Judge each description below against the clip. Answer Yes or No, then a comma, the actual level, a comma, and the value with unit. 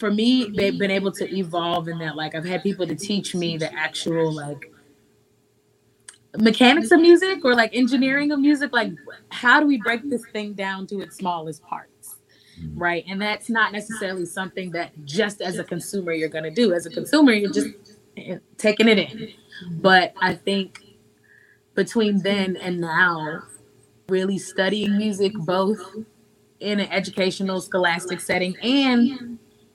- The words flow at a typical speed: Yes, average, 155 wpm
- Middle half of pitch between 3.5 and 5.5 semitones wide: Yes, average, 3.8 semitones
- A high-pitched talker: Yes, high, 195 Hz